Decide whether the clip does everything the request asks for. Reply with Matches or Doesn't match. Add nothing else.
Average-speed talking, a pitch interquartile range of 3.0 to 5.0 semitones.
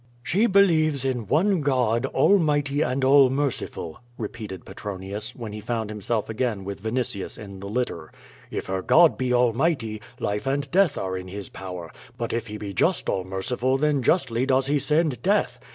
Doesn't match